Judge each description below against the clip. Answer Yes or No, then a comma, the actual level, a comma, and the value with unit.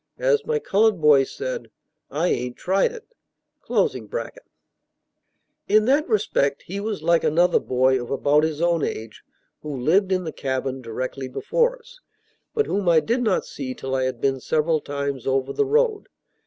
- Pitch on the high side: No, medium, 165 Hz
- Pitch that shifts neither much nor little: No, wide, 8.7 semitones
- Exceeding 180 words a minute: No, average, 165 wpm